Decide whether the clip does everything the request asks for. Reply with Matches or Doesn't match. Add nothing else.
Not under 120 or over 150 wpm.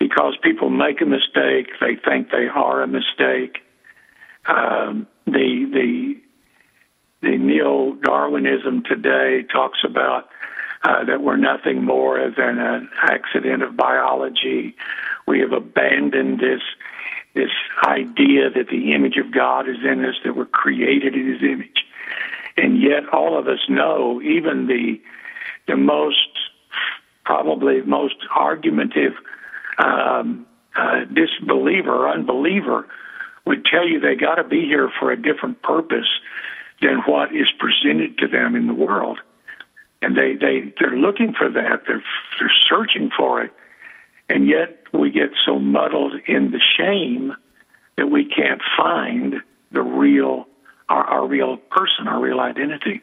Matches